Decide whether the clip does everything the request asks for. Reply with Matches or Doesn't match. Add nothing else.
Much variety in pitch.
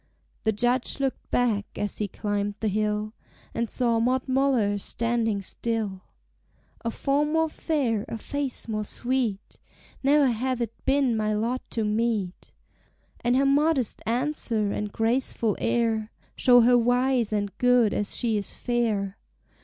Doesn't match